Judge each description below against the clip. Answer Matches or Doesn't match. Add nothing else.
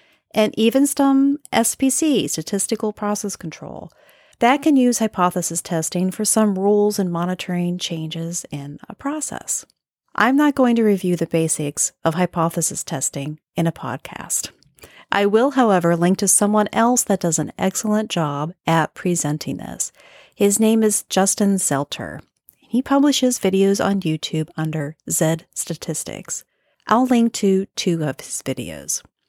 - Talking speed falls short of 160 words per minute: Matches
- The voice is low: Doesn't match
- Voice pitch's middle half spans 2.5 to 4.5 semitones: Doesn't match